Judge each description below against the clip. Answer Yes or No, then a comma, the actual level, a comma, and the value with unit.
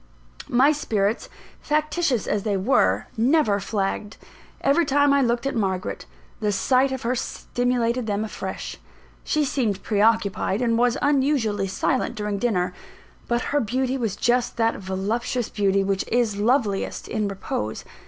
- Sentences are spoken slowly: No, average, 145 wpm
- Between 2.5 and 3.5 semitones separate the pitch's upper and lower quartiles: No, average, 4.3 semitones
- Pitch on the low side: No, high, 230 Hz